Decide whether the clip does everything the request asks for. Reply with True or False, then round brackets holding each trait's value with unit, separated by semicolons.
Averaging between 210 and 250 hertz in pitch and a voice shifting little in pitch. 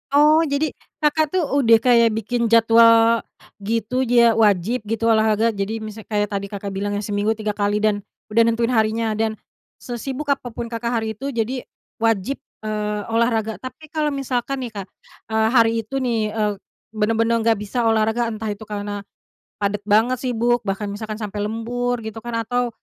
True (225 Hz; 2.2 semitones)